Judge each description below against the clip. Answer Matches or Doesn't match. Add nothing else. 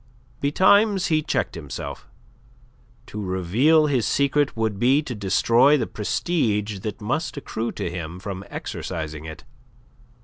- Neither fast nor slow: Doesn't match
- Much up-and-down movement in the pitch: Matches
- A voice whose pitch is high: Doesn't match